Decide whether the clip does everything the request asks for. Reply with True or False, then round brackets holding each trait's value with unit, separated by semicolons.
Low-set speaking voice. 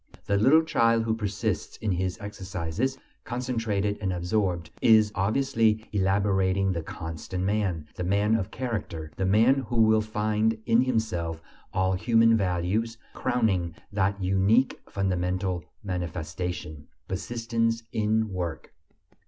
True (100 Hz)